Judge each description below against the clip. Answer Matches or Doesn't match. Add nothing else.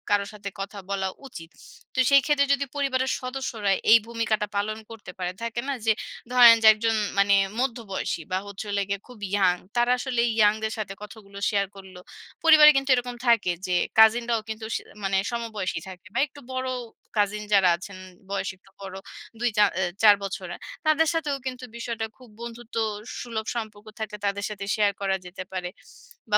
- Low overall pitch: Doesn't match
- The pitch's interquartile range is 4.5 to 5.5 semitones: Doesn't match